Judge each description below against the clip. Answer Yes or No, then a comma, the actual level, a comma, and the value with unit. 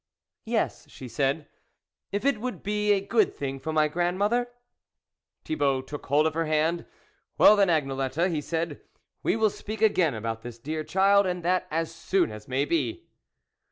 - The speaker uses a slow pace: No, average, 185 wpm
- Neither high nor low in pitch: Yes, medium, 160 Hz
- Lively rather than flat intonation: Yes, wide, 5.8 semitones